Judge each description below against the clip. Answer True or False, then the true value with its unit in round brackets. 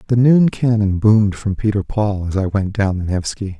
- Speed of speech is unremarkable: False (215 wpm)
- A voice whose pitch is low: True (105 Hz)